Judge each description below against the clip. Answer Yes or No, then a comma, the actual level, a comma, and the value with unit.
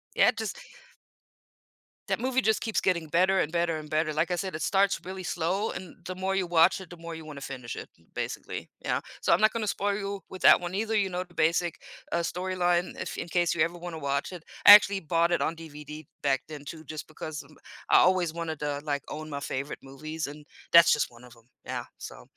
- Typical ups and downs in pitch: Yes, average, 3.5 semitones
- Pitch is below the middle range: No, medium, 170 Hz